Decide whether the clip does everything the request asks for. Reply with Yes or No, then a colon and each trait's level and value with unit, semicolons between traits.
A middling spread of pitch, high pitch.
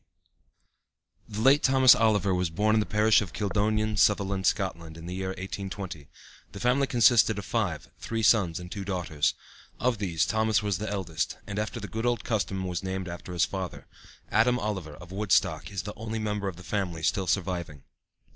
No: average, 3.2 semitones; low, 100 Hz